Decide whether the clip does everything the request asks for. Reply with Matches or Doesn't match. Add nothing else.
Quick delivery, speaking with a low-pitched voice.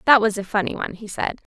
Doesn't match